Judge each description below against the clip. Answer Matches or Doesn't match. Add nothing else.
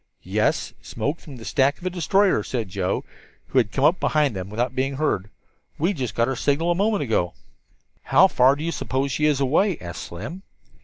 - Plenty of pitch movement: Matches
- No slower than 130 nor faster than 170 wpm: Doesn't match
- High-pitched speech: Doesn't match